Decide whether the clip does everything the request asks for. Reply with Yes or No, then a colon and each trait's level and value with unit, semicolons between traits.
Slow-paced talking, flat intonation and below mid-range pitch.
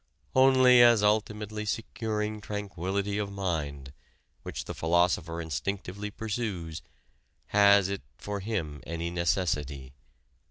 No: slow, 105 wpm; average, 4.1 semitones; low, 100 Hz